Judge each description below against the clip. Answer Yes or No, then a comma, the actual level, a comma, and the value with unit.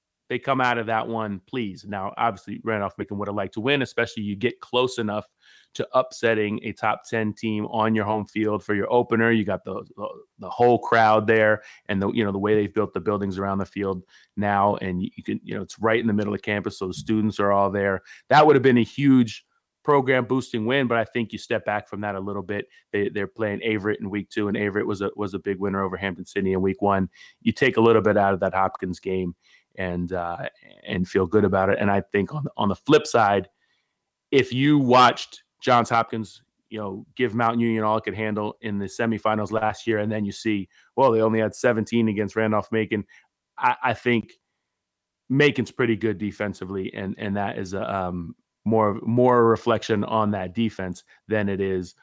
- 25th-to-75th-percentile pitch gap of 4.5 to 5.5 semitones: No, narrow, 2.4 semitones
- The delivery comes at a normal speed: No, fast, 225 wpm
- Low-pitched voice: Yes, low, 105 Hz